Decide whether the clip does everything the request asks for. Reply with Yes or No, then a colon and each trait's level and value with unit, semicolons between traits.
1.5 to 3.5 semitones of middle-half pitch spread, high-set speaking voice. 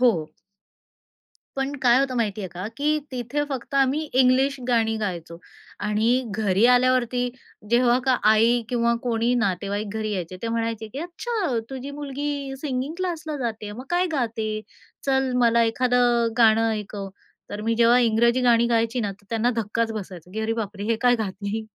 Yes: average, 2.9 semitones; high, 235 Hz